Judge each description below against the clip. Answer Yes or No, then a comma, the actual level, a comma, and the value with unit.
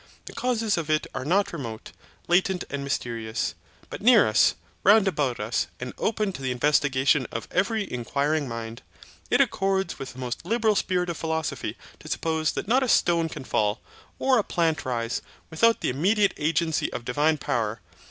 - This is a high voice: No, medium, 155 Hz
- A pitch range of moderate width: No, wide, 7.3 semitones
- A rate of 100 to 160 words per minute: No, average, 175 wpm